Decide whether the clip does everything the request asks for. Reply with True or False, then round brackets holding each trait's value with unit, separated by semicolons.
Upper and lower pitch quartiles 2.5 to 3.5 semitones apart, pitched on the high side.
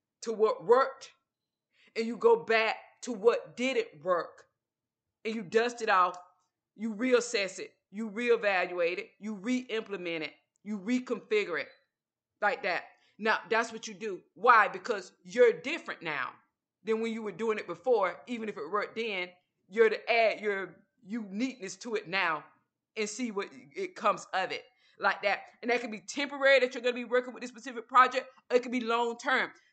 True (3.0 semitones; 230 Hz)